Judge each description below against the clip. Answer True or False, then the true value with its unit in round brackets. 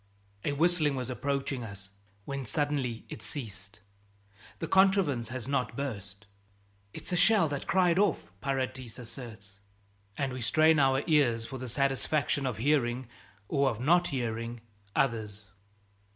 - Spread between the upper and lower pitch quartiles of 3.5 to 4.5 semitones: True (4.0 semitones)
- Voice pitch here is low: True (130 Hz)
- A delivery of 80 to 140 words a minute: True (135 wpm)